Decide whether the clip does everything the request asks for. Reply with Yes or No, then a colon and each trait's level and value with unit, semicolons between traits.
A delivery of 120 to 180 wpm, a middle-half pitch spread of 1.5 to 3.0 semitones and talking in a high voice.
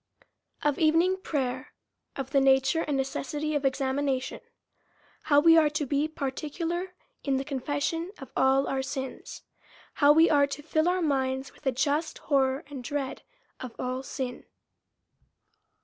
Yes: average, 150 wpm; narrow, 2.6 semitones; very high, 280 Hz